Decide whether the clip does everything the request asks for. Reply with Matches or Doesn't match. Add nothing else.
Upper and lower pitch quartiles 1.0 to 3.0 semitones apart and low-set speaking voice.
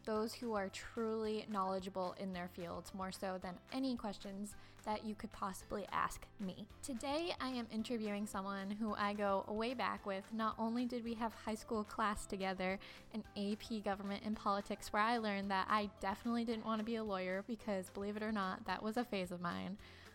Doesn't match